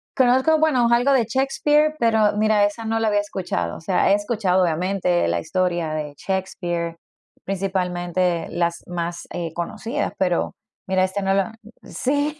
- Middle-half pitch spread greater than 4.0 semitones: Yes, average, 4.6 semitones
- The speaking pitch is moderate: No, high, 195 Hz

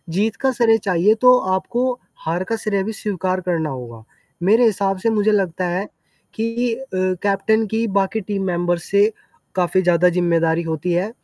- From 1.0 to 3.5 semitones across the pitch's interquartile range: No, average, 4.0 semitones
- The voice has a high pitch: Yes, high, 195 Hz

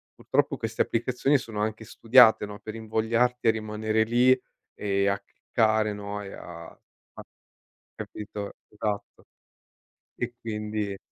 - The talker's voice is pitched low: Yes, low, 110 Hz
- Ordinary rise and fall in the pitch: No, narrow, 1.8 semitones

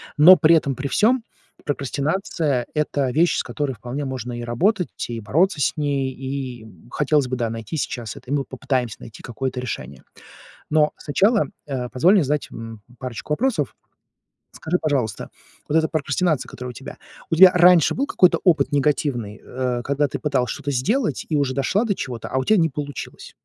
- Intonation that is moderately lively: Yes, average, 4.1 semitones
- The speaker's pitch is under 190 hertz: Yes, medium, 140 Hz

